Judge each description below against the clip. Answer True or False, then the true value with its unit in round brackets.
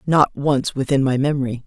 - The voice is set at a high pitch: False (135 Hz)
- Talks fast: False (180 wpm)